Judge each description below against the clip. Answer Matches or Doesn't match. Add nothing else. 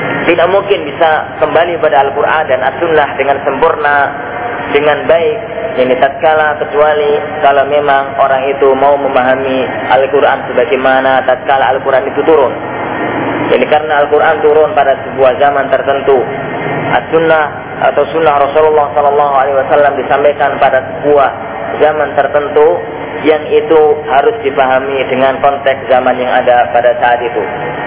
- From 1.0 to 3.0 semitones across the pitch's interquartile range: Matches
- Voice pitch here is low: Doesn't match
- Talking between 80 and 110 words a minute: Doesn't match